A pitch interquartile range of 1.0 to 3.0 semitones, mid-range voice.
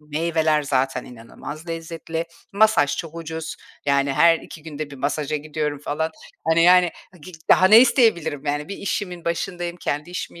Yes: average, 2.7 semitones; medium, 160 Hz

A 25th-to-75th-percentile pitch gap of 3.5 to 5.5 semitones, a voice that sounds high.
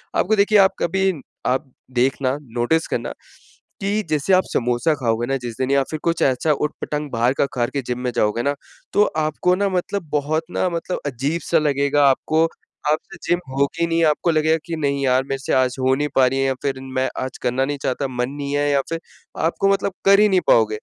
No: average, 4.1 semitones; medium, 145 Hz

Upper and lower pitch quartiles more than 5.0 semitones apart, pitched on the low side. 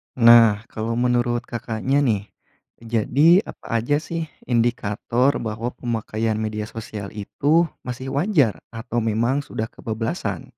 No: average, 2.9 semitones; low, 115 Hz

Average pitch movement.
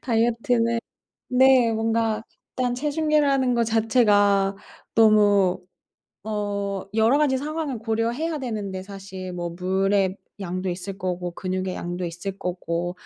Yes: average, 4.3 semitones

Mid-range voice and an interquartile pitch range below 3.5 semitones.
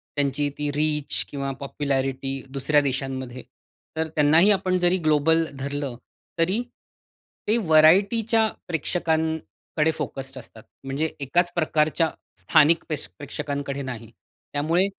Yes: medium, 150 Hz; average, 3.0 semitones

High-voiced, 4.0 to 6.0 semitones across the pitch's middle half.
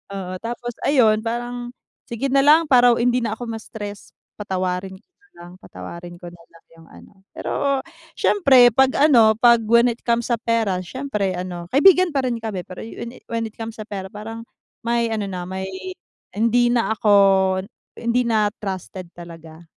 Yes: high, 225 Hz; average, 4.4 semitones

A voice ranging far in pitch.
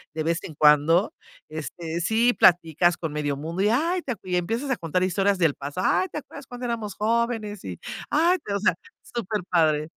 Yes: wide, 6.1 semitones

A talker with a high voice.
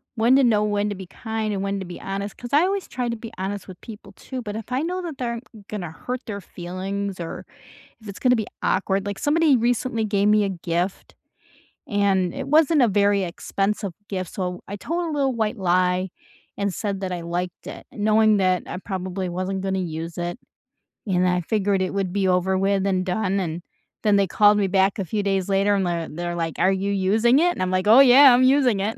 Yes: high, 200 Hz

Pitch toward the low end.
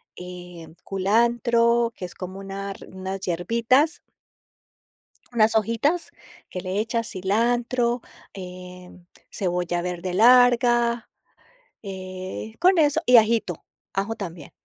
No: high, 205 Hz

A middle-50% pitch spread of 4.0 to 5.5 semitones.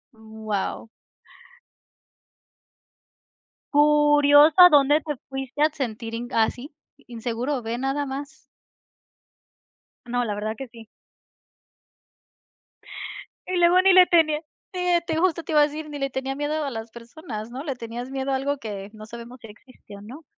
Yes: average, 4.4 semitones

